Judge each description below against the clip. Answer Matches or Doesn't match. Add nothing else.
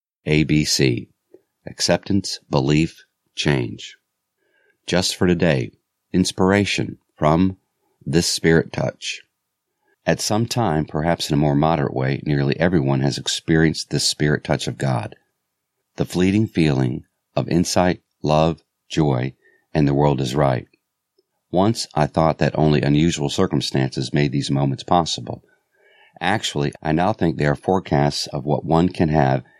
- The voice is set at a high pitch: Doesn't match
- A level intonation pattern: Doesn't match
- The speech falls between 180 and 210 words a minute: Doesn't match